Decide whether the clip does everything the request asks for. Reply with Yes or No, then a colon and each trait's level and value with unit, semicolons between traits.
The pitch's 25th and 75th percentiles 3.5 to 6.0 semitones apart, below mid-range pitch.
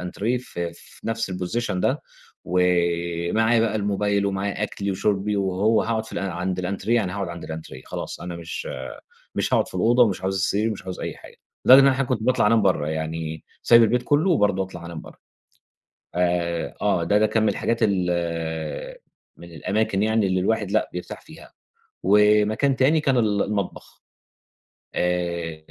Yes: average, 3.8 semitones; low, 100 Hz